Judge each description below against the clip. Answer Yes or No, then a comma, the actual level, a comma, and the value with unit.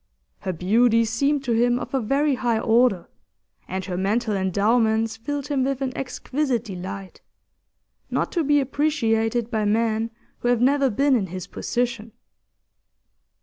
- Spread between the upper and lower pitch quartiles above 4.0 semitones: No, average, 3.7 semitones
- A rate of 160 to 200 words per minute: No, average, 150 wpm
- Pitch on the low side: No, high, 230 Hz